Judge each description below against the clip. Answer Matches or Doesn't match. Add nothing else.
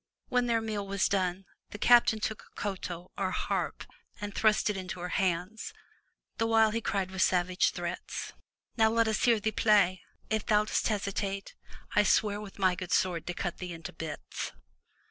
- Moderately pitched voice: Doesn't match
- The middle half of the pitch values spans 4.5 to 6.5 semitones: Doesn't match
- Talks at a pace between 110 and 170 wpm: Doesn't match